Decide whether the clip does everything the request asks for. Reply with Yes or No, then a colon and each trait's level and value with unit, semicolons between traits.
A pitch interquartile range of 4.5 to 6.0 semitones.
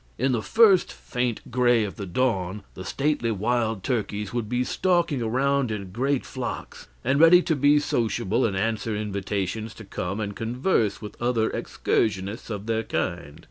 No: average, 3.8 semitones